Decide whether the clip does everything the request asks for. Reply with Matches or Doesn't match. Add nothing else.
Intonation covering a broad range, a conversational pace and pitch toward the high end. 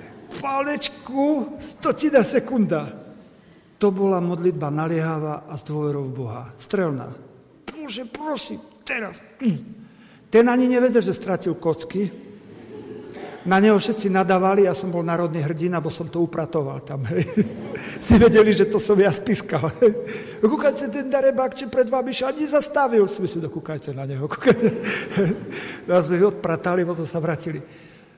Matches